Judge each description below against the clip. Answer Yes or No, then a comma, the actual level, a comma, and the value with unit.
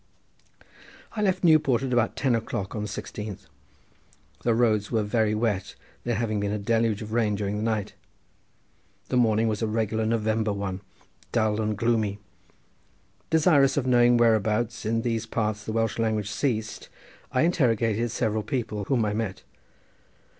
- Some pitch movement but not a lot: No, narrow, 2.0 semitones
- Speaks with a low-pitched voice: Yes, low, 110 Hz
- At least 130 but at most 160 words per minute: Yes, average, 155 wpm